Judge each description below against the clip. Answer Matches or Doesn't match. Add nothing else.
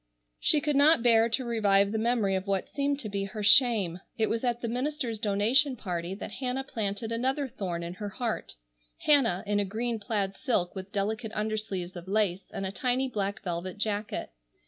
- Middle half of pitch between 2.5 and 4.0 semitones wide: Matches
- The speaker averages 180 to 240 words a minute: Matches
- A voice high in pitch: Matches